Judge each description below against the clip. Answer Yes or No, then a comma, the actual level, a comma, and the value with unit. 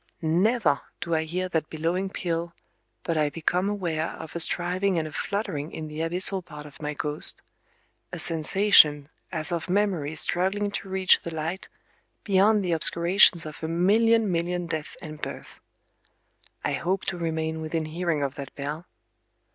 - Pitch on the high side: No, medium, 170 Hz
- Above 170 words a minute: No, average, 160 wpm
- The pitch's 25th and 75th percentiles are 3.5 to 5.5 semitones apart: No, average, 3.1 semitones